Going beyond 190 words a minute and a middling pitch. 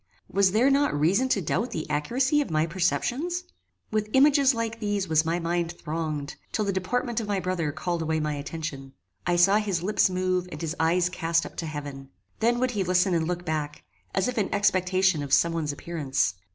Yes: fast, 205 wpm; medium, 180 Hz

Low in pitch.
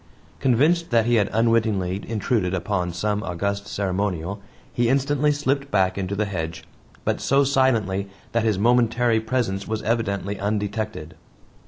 Yes: low, 105 Hz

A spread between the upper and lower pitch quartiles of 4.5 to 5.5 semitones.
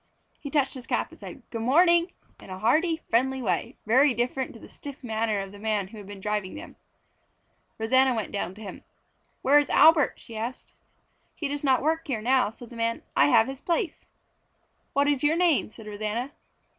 Yes: average, 4.9 semitones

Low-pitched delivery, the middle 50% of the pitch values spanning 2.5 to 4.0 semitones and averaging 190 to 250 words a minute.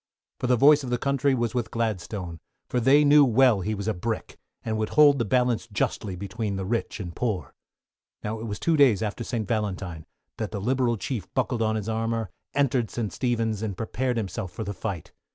Yes: low, 115 Hz; average, 3.4 semitones; fast, 205 wpm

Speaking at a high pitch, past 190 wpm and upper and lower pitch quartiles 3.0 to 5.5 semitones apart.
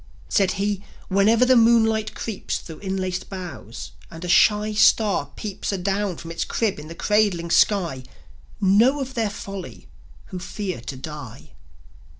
No: high, 195 Hz; average, 150 wpm; average, 3.7 semitones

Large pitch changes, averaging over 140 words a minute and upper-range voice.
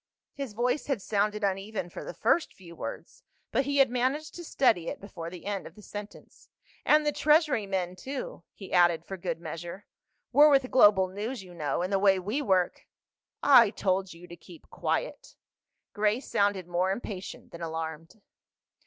Yes: wide, 5.8 semitones; average, 180 wpm; high, 200 Hz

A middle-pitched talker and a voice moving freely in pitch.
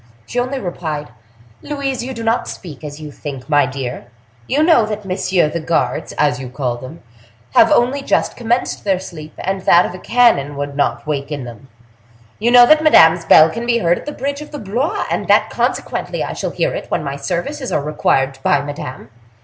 Yes: medium, 170 Hz; wide, 8.9 semitones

